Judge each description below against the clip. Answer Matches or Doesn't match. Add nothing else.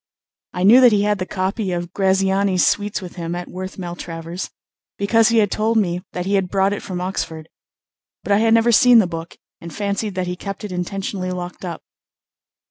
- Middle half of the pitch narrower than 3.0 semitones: Matches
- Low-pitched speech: Doesn't match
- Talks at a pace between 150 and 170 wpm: Doesn't match